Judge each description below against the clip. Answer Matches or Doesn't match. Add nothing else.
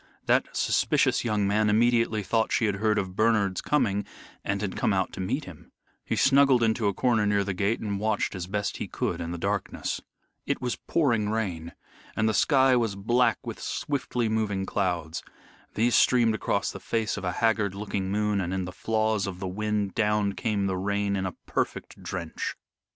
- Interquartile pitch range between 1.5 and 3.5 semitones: Matches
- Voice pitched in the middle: Doesn't match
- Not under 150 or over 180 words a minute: Doesn't match